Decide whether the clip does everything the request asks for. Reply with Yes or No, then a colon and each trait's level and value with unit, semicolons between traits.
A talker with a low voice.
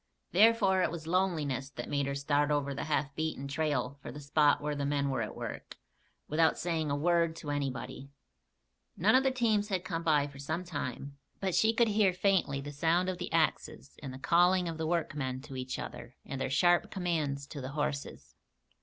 No: medium, 150 Hz